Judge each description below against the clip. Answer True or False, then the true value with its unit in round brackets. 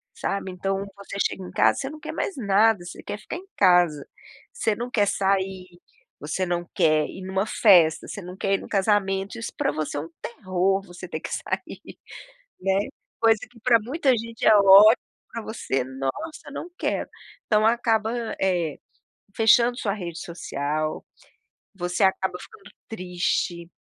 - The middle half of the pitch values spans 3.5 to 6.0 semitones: True (4.0 semitones)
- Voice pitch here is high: True (195 Hz)